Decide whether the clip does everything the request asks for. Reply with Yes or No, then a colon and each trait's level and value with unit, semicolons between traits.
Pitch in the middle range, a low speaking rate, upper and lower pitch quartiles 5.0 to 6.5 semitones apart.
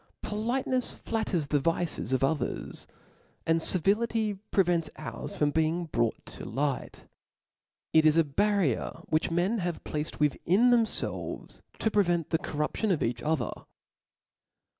Yes: medium, 165 Hz; slow, 130 wpm; wide, 5.5 semitones